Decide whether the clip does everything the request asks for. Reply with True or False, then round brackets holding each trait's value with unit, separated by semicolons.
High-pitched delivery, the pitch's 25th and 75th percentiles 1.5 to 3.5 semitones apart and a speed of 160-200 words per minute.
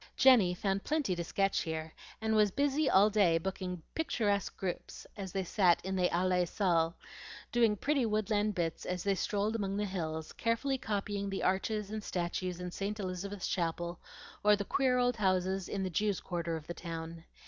True (195 Hz; 3.1 semitones; 180 wpm)